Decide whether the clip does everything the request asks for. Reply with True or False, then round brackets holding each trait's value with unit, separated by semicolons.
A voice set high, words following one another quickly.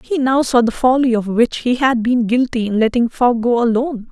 True (240 Hz; 235 wpm)